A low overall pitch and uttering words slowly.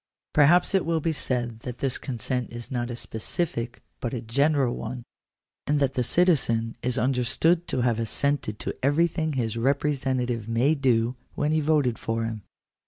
No: low, 125 Hz; average, 170 wpm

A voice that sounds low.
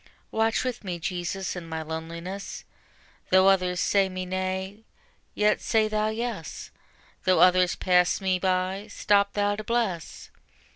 No: high, 190 Hz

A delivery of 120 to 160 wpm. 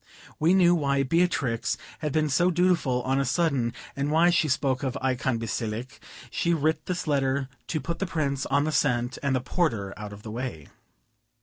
No: average, 190 wpm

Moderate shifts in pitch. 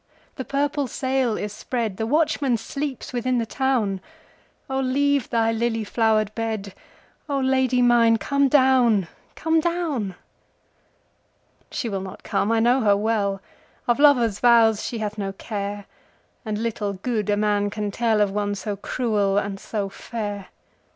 Yes: average, 4.1 semitones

